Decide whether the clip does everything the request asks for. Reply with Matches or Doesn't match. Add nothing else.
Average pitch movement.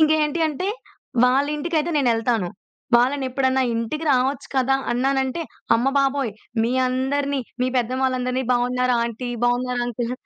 Doesn't match